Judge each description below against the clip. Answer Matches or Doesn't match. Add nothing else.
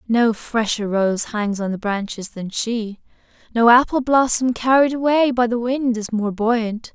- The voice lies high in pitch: Matches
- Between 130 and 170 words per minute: Matches